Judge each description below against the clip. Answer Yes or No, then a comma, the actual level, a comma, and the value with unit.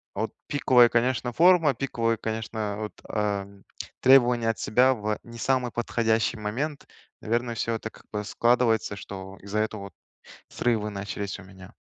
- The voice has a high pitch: No, low, 115 Hz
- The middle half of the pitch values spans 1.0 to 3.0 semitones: Yes, average, 2.7 semitones